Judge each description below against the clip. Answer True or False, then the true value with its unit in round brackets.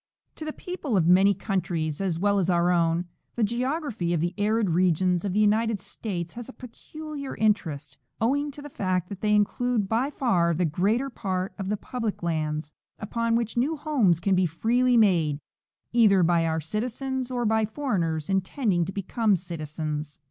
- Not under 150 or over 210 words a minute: True (180 wpm)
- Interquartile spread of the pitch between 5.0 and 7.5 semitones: True (5.5 semitones)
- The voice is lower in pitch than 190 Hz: False (200 Hz)